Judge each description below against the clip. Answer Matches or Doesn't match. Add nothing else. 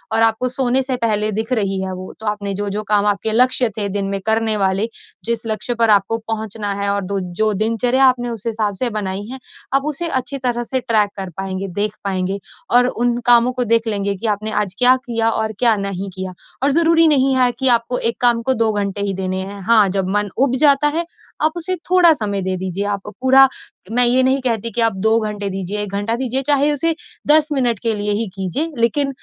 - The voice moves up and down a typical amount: Matches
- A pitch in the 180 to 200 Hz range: Doesn't match